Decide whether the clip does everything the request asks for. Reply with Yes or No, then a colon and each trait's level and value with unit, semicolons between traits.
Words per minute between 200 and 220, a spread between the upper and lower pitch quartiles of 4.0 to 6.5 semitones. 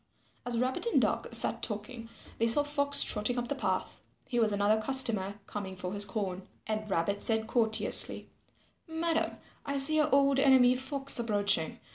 No: average, 165 wpm; average, 4.9 semitones